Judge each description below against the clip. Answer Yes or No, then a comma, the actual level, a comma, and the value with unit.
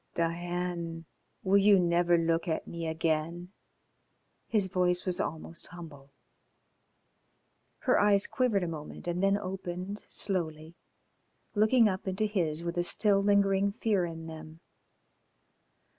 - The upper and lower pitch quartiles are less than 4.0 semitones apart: Yes, average, 3.0 semitones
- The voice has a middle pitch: Yes, medium, 175 Hz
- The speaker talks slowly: Yes, slow, 125 wpm